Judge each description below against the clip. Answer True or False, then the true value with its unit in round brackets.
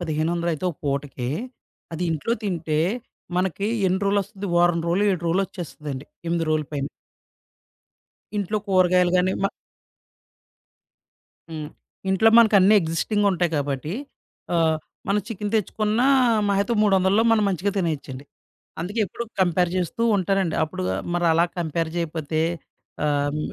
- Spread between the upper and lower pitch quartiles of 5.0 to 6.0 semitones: False (3.8 semitones)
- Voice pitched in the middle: True (175 Hz)